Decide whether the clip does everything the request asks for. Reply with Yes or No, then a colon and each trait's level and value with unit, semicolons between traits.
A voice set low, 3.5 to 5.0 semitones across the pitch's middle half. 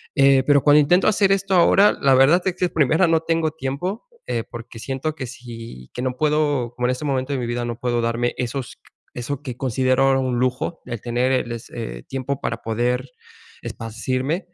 Yes: low, 130 Hz; average, 3.8 semitones